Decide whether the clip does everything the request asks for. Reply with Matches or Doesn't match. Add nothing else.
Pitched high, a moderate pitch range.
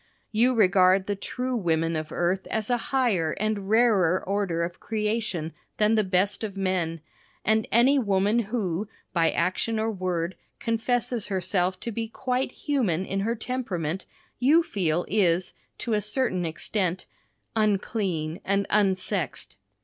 Matches